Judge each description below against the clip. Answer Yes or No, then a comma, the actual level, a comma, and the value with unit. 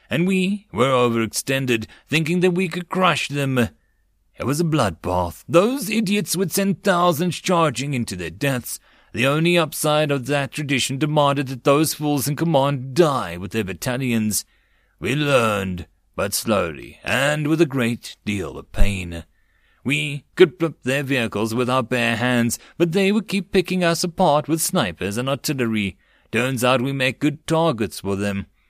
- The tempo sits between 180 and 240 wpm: No, average, 165 wpm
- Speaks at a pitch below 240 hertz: Yes, low, 135 Hz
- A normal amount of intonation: No, wide, 6.5 semitones